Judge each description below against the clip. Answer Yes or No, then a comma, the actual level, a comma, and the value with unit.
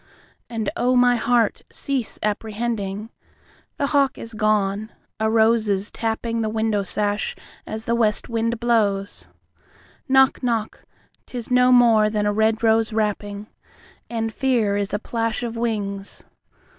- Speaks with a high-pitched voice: Yes, high, 225 Hz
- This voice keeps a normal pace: No, slow, 125 wpm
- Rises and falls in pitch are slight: Yes, narrow, 2.0 semitones